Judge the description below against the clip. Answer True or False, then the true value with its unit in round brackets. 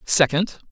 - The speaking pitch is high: False (170 Hz)